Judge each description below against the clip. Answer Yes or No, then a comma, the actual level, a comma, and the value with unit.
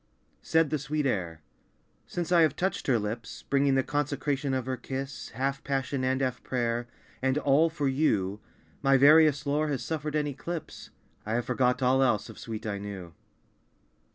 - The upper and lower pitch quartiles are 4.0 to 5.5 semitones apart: No, average, 3.4 semitones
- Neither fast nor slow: Yes, average, 175 wpm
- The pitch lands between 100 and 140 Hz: Yes, low, 135 Hz